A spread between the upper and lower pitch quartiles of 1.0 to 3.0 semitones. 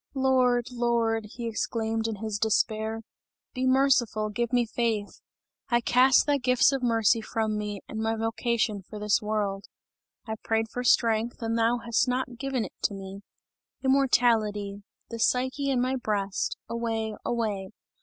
Yes: narrow, 2.4 semitones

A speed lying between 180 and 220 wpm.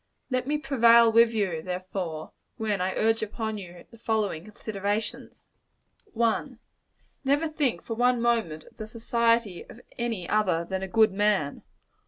No: average, 150 wpm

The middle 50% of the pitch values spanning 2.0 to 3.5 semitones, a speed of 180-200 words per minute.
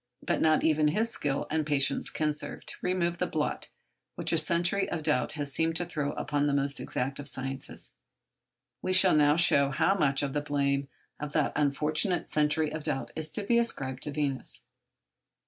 Yes: narrow, 2.6 semitones; average, 195 wpm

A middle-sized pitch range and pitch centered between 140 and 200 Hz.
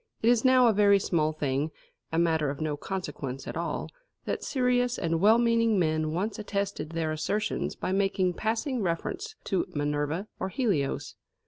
No: wide, 6.2 semitones; high, 190 Hz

